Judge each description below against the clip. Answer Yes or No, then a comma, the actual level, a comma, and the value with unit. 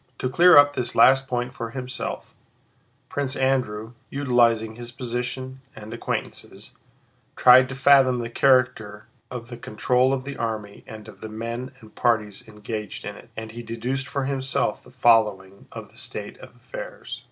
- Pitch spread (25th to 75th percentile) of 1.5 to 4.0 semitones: Yes, average, 2.8 semitones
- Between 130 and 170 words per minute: Yes, average, 165 wpm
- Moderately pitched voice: No, low, 120 Hz